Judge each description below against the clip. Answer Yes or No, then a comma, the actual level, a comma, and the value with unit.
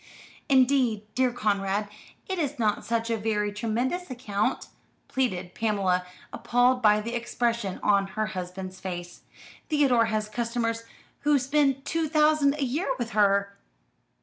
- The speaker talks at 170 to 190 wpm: No, slow, 135 wpm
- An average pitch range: Yes, average, 4.1 semitones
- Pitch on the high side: Yes, high, 230 Hz